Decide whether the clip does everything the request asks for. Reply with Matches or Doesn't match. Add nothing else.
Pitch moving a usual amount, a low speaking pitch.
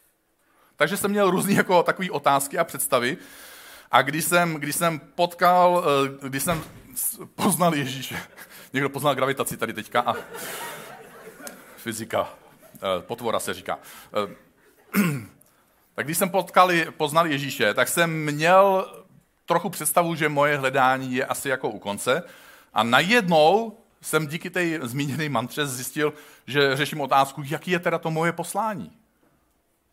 Doesn't match